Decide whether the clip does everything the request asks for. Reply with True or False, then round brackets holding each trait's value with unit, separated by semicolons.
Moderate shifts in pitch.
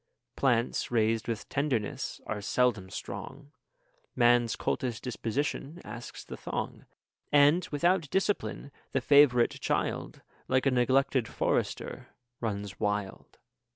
True (4.0 semitones)